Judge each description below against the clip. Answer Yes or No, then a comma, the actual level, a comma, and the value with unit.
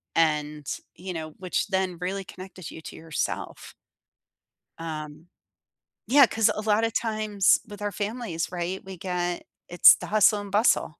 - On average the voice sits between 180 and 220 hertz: Yes, medium, 185 Hz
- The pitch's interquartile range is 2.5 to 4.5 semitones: Yes, average, 4.0 semitones